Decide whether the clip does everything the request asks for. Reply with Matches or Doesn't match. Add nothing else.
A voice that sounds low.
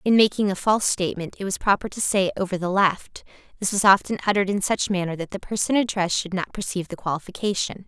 Doesn't match